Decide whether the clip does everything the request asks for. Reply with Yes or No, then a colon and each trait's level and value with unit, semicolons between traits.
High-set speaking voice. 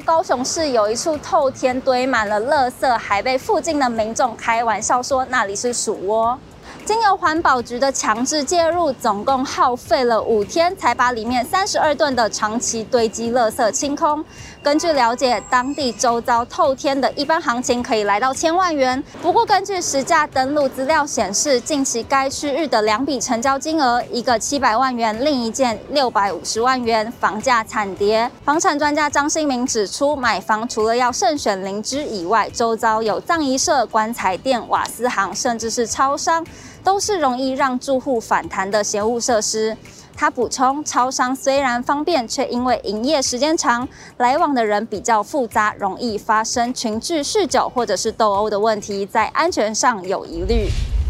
Yes: very high, 250 Hz